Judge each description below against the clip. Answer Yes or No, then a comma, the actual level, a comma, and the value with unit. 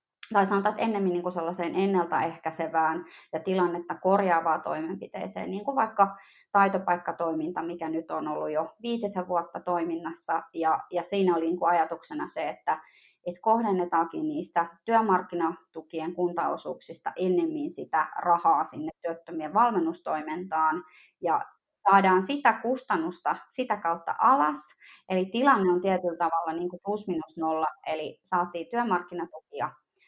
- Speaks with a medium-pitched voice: Yes, medium, 175 Hz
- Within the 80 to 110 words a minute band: No, average, 125 wpm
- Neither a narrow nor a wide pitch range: Yes, average, 3.3 semitones